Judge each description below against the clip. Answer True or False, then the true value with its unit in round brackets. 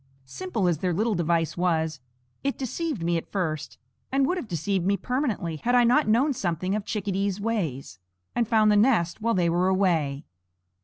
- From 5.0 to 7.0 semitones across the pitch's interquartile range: True (5.3 semitones)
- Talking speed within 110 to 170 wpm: False (185 wpm)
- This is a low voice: False (190 Hz)